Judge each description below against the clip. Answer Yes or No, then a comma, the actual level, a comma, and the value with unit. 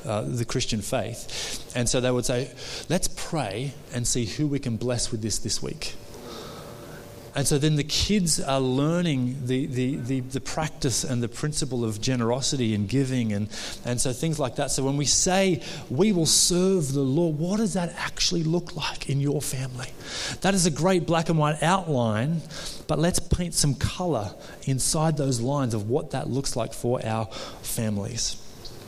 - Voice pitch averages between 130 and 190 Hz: Yes, low, 135 Hz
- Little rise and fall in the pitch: No, average, 4.7 semitones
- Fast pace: No, average, 185 wpm